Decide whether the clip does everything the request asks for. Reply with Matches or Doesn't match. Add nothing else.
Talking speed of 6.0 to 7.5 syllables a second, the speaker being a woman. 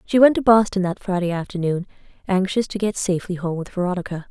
Matches